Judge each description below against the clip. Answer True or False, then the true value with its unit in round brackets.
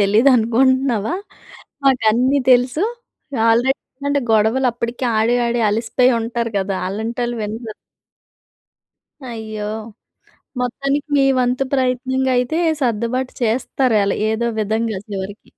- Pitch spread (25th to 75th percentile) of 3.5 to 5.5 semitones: False (2.9 semitones)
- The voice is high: True (240 Hz)